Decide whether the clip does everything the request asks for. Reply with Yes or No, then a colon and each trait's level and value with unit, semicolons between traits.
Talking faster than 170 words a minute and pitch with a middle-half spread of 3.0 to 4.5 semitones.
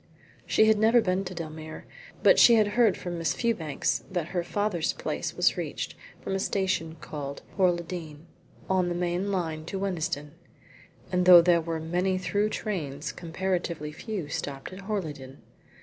No: average, 165 wpm; average, 3.3 semitones